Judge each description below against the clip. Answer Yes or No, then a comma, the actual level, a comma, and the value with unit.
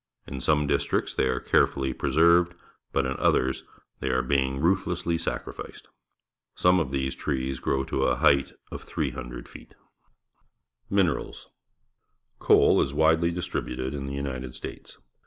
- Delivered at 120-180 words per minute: Yes, average, 140 wpm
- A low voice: Yes, very low, 70 Hz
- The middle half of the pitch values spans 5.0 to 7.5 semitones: No, average, 3.8 semitones